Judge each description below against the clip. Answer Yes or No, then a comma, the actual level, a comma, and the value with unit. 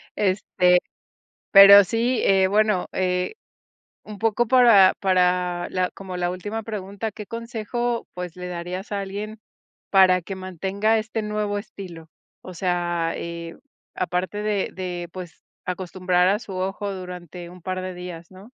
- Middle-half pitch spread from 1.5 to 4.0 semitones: Yes, narrow, 2.6 semitones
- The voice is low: No, medium, 185 Hz